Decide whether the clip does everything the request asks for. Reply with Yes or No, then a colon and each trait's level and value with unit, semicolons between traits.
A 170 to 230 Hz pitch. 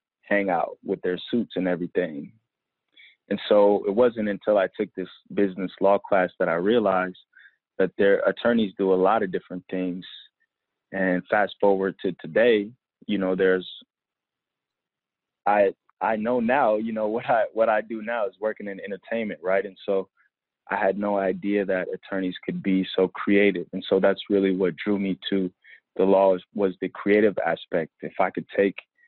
No: low, 100 Hz